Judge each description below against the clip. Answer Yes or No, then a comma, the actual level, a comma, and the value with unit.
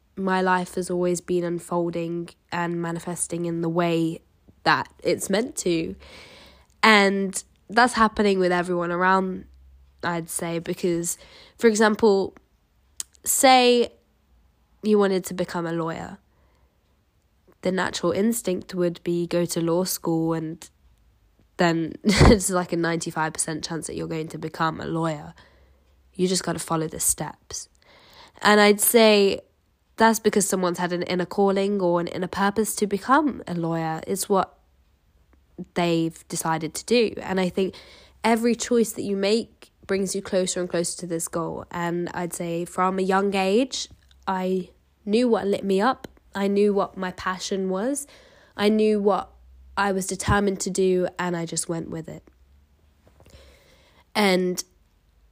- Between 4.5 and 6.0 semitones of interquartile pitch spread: No, average, 3.1 semitones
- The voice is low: No, medium, 180 Hz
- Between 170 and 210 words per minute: No, average, 150 wpm